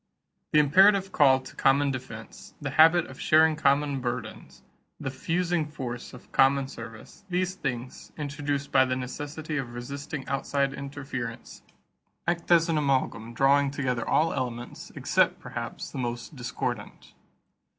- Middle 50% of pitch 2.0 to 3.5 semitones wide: Yes, average, 3.2 semitones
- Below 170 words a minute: Yes, average, 140 wpm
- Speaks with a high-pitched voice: No, medium, 140 Hz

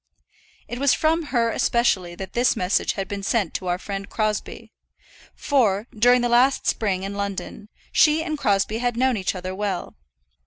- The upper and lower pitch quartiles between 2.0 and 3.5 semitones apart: No, average, 4.0 semitones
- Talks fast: No, average, 170 wpm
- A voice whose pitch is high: Yes, high, 215 Hz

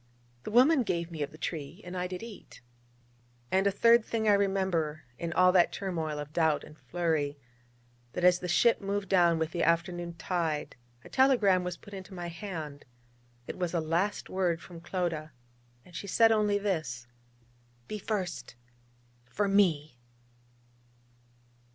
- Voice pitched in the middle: Yes, medium, 180 Hz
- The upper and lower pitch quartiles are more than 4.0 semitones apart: No, average, 3.6 semitones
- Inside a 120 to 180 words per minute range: Yes, average, 160 wpm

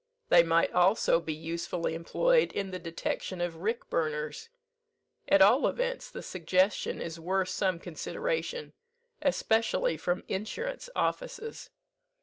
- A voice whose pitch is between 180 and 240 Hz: Yes, medium, 185 Hz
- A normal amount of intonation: No, wide, 8.9 semitones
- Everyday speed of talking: No, slow, 125 wpm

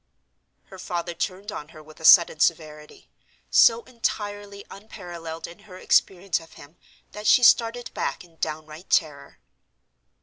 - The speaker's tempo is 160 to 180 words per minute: No, average, 140 wpm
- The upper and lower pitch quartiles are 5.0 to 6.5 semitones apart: No, average, 4.5 semitones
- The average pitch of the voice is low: No, medium, 175 Hz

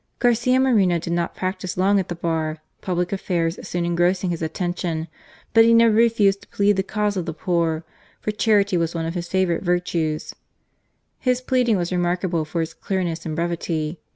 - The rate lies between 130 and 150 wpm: No, average, 180 wpm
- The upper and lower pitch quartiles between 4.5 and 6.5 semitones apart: No, average, 3.2 semitones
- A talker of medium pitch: Yes, medium, 180 Hz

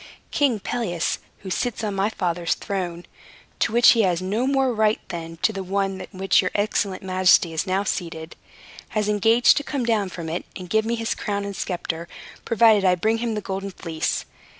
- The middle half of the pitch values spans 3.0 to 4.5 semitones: Yes, average, 3.5 semitones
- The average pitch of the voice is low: No, high, 195 Hz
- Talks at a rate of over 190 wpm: Yes, average, 200 wpm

